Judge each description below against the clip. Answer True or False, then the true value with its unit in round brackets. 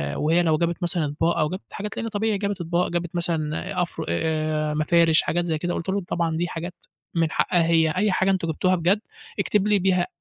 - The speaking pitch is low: False (170 Hz)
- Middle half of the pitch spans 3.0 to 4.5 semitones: False (2.5 semitones)